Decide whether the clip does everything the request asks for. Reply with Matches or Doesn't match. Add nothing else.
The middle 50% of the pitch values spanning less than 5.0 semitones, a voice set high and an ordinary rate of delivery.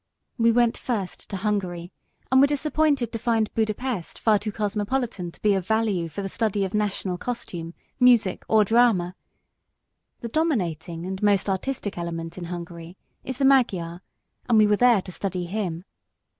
Matches